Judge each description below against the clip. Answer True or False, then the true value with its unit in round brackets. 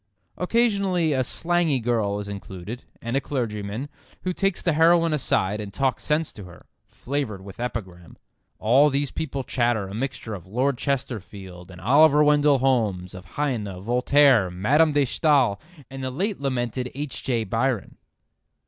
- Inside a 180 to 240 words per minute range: False (155 wpm)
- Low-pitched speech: True (125 Hz)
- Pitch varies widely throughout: True (6.0 semitones)